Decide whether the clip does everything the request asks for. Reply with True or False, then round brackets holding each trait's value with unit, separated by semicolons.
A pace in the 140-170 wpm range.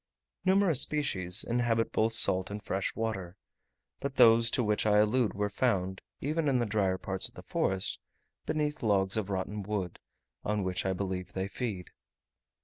True (165 wpm)